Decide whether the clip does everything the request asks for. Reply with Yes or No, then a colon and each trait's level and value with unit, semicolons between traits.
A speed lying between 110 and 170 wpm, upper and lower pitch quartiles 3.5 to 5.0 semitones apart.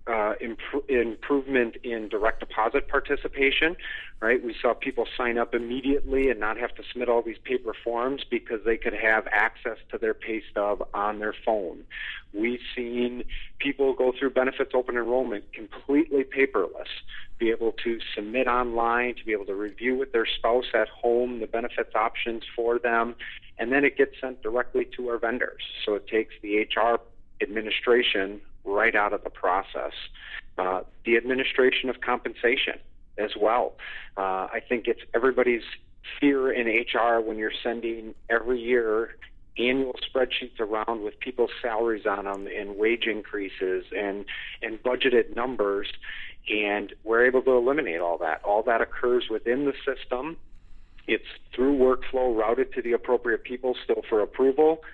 No: average, 155 wpm; average, 2.9 semitones